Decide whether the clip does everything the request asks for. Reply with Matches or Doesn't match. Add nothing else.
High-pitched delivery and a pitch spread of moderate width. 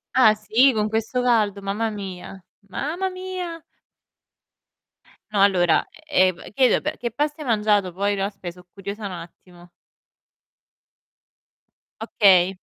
Matches